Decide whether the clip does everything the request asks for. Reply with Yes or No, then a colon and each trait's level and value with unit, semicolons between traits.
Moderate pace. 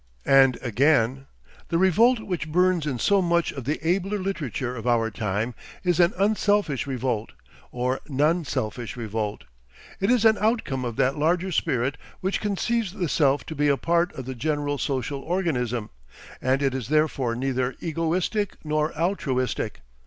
Yes: average, 160 wpm